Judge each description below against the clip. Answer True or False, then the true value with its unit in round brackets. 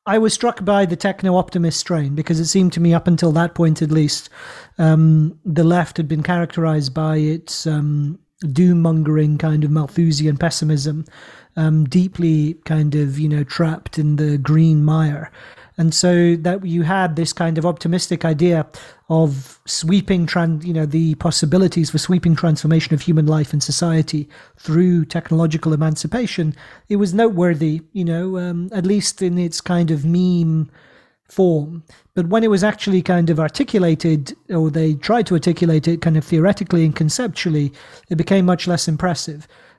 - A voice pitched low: False (165 Hz)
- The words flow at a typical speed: True (165 wpm)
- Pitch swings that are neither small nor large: False (2.3 semitones)